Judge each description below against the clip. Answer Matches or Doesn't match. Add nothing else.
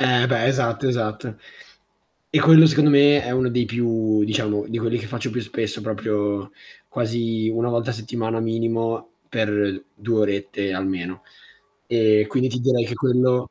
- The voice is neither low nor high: Doesn't match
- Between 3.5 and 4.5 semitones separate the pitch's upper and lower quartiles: Doesn't match